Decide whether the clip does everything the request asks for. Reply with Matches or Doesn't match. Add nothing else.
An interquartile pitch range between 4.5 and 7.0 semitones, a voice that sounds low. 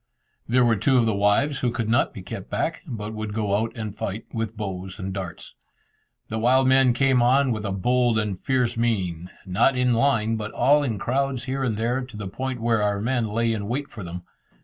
Doesn't match